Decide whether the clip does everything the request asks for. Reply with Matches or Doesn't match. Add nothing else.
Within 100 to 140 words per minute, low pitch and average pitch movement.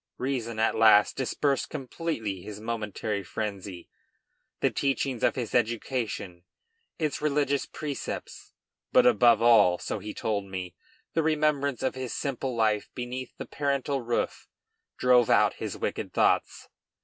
Matches